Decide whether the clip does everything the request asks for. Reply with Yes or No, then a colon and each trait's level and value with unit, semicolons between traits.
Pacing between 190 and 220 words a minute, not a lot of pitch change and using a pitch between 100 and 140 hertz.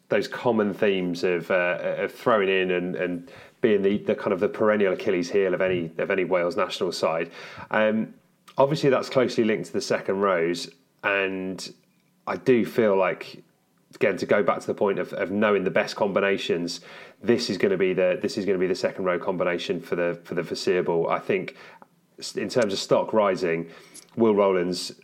No: average, 195 wpm; narrow, 2.0 semitones; very low, 90 Hz